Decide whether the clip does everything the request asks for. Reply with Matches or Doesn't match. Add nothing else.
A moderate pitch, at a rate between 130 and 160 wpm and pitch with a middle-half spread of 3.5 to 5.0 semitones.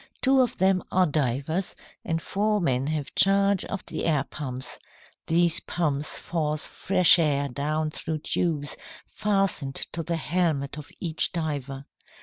Matches